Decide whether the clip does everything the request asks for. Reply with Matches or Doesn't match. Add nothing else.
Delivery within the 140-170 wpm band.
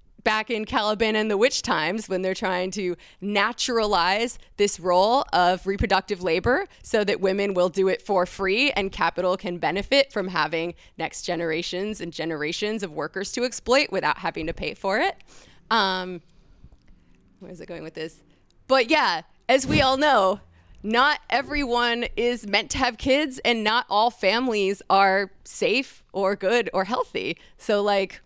Matches